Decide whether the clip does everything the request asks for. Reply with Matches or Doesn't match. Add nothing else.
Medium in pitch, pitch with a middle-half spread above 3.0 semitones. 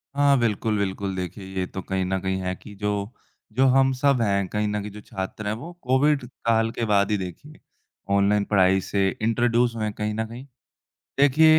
Doesn't match